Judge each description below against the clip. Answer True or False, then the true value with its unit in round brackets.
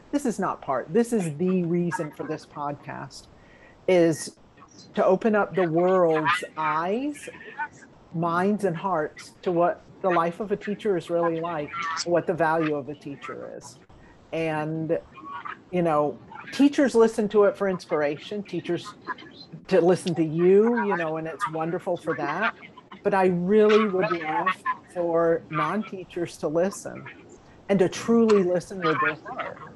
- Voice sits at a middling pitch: True (180 Hz)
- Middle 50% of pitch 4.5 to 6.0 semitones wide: False (3.8 semitones)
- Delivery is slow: False (150 wpm)